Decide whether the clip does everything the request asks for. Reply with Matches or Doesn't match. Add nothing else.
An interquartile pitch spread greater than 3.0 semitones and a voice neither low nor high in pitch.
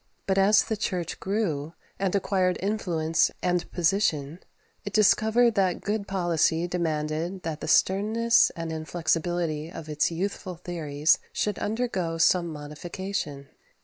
Matches